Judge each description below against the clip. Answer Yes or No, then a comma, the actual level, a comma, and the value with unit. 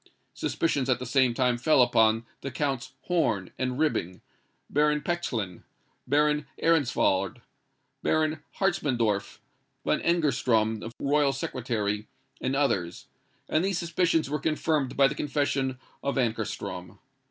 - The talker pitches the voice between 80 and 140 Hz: Yes, low, 135 Hz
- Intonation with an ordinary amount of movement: Yes, average, 4.5 semitones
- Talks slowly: Yes, slow, 120 wpm